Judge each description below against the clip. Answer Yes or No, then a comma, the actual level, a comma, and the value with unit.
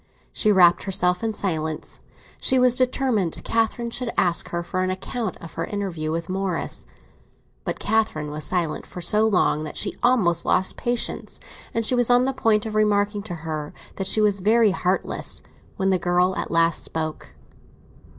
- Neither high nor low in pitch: No, high, 195 Hz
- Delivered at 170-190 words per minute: Yes, average, 175 wpm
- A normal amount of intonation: Yes, average, 4.4 semitones